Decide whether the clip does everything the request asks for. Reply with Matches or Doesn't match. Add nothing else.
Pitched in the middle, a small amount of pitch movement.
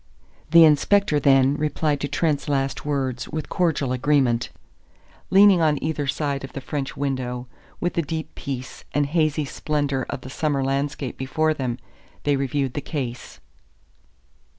Matches